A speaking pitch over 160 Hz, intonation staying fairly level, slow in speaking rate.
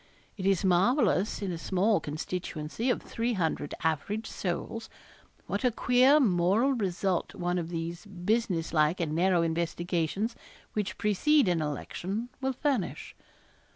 No: medium, 185 Hz; average, 4.8 semitones; slow, 130 wpm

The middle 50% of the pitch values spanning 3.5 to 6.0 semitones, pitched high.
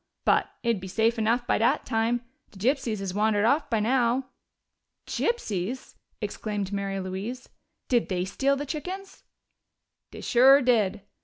Yes: average, 4.1 semitones; high, 230 Hz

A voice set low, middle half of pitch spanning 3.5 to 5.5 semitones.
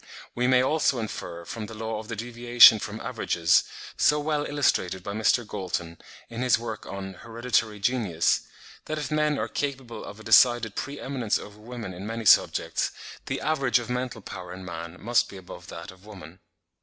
Yes: low, 110 Hz; average, 4.4 semitones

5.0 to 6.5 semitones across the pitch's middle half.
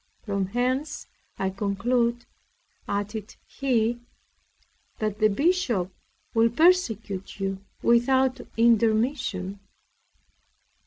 No: average, 3.9 semitones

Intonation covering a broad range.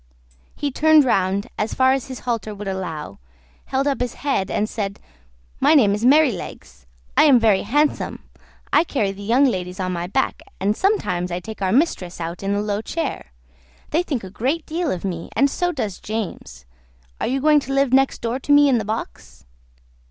Yes: wide, 6.3 semitones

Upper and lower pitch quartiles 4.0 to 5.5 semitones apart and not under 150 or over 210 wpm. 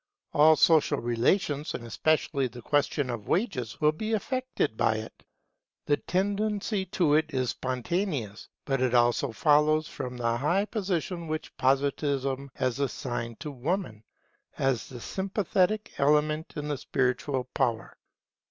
No: average, 5.1 semitones; slow, 135 wpm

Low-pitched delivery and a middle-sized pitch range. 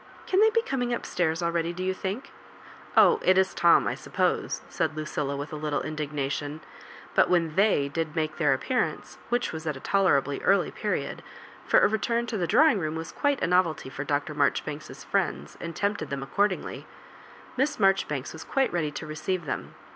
No: medium, 165 Hz; average, 5.0 semitones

